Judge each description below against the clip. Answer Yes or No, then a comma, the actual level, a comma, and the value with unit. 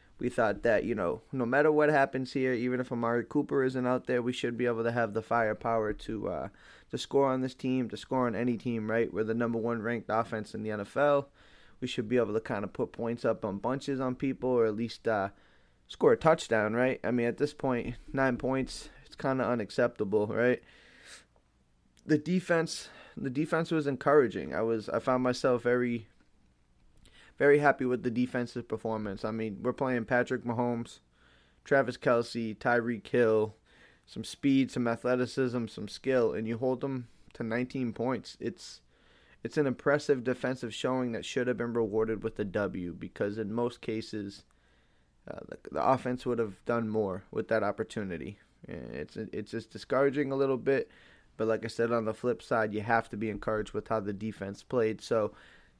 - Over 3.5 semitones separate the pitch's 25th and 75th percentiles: No, average, 2.8 semitones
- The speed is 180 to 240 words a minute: Yes, average, 185 wpm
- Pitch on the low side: Yes, low, 120 Hz